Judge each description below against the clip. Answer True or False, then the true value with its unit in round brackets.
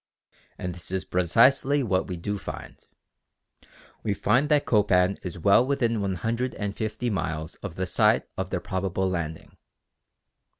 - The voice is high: False (100 Hz)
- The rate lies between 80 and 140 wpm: True (135 wpm)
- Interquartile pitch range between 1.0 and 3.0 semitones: False (4.2 semitones)